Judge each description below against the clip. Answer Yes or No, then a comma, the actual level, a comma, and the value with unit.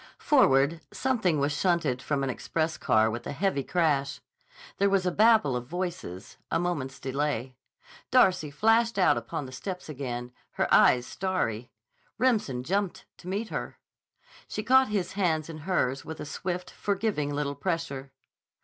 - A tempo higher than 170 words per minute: No, average, 155 wpm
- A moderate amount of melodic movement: No, wide, 5.9 semitones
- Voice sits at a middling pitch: Yes, medium, 160 Hz